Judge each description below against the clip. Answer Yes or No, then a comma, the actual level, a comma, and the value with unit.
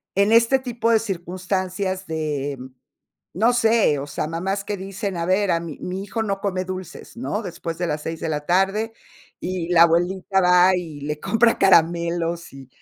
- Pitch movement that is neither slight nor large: Yes, average, 3.2 semitones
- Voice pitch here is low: No, medium, 185 Hz